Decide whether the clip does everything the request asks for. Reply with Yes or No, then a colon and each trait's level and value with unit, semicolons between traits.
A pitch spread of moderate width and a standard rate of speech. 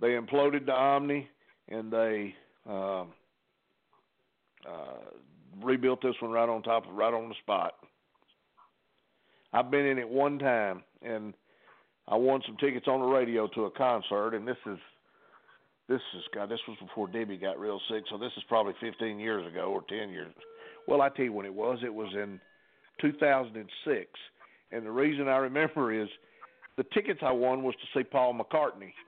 Yes: average, 3.6 semitones; average, 175 wpm